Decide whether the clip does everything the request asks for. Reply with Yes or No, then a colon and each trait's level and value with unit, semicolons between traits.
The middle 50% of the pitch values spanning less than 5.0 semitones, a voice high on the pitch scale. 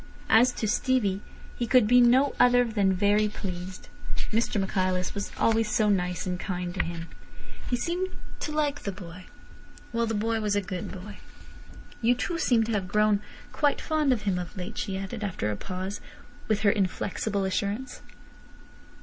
Yes: average, 3.7 semitones; high, 210 Hz